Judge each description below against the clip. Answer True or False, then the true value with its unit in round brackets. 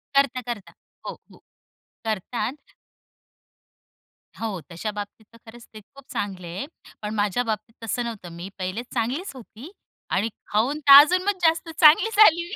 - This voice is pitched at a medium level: False (230 Hz)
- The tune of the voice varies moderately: False (5.8 semitones)